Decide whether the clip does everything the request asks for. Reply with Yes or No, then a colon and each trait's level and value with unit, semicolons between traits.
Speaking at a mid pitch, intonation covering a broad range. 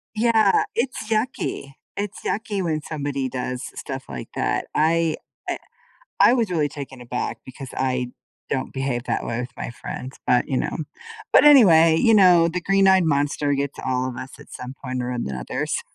Yes: medium, 145 Hz; wide, 6.7 semitones